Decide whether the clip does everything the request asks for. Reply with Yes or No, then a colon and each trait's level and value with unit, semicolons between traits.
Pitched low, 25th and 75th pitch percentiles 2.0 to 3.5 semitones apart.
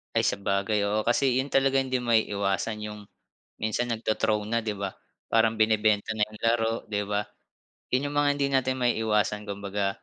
Yes: low, 110 Hz; narrow, 2.6 semitones